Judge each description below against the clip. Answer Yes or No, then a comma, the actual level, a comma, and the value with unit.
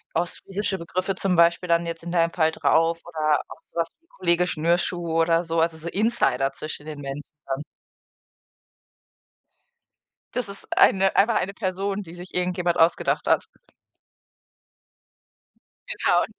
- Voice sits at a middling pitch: Yes, medium, 170 Hz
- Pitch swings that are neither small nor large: No, narrow, 2.3 semitones